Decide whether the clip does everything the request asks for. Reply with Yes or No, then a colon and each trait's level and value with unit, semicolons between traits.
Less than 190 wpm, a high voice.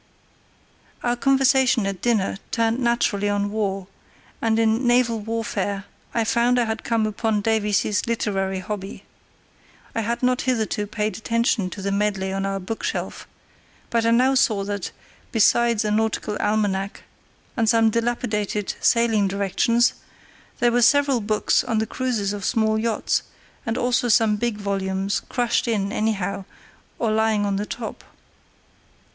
Yes: average, 145 wpm; high, 220 Hz